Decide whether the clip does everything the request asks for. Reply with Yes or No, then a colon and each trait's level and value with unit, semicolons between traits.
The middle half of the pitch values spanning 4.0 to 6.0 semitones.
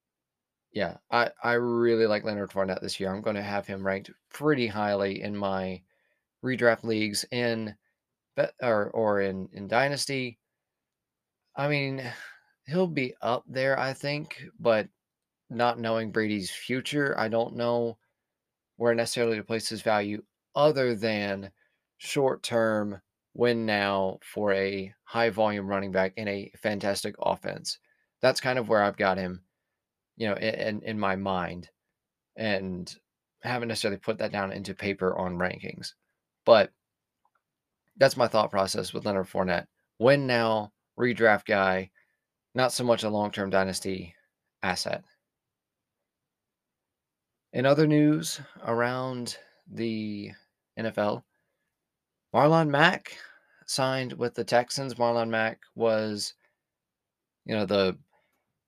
No: average, 3.4 semitones